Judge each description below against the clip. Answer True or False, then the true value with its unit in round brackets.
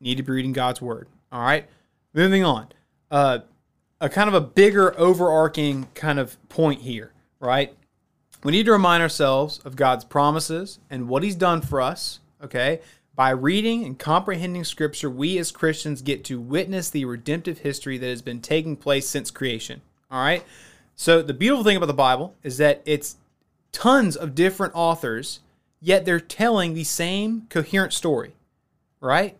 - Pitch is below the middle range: False (155 Hz)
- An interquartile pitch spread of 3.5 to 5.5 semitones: True (4.8 semitones)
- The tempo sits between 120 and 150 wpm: False (165 wpm)